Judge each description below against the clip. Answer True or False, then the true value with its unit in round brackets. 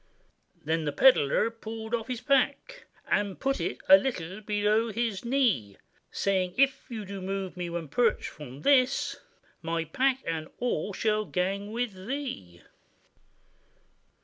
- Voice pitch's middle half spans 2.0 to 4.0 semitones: False (5.5 semitones)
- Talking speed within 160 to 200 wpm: False (145 wpm)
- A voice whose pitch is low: False (210 Hz)